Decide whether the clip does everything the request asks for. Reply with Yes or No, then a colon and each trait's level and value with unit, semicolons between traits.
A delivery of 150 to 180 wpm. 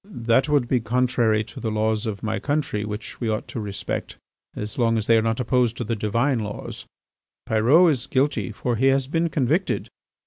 No: average, 200 wpm